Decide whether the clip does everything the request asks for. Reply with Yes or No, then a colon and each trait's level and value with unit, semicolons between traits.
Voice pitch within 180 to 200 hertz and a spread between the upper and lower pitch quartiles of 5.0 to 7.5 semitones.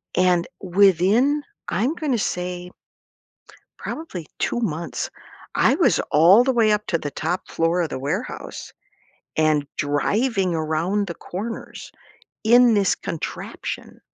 Yes: medium, 185 Hz; wide, 5.4 semitones